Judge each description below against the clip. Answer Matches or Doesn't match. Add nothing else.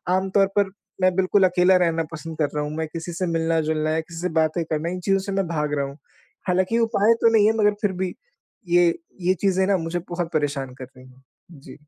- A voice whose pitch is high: Doesn't match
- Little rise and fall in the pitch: Doesn't match